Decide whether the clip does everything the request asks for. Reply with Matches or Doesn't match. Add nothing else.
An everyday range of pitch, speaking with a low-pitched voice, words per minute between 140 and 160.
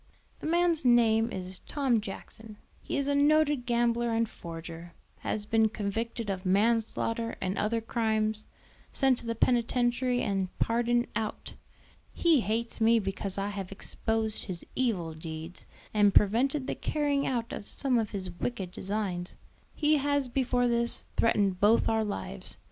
Doesn't match